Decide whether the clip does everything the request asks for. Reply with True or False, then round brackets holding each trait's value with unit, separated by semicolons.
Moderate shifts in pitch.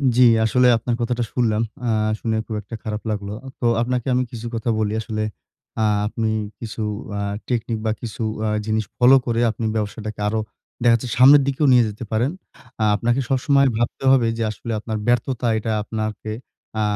False (2.2 semitones)